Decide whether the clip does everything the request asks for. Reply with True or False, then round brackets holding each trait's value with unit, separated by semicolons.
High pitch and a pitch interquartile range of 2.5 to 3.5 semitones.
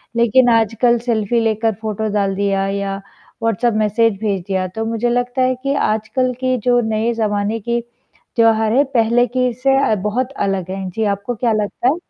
True (225 Hz; 2.9 semitones)